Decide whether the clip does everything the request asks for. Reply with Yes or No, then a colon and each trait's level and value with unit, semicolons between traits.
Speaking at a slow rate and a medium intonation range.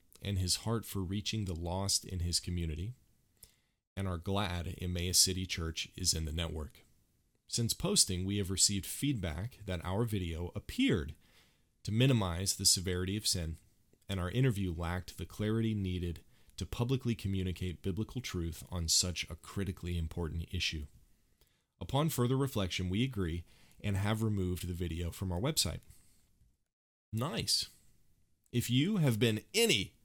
No: average, 145 wpm; average, 3.7 semitones